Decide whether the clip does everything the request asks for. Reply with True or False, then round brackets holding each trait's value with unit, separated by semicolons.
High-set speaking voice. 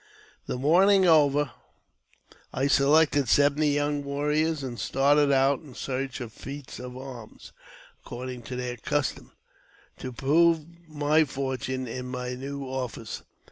False (140 Hz)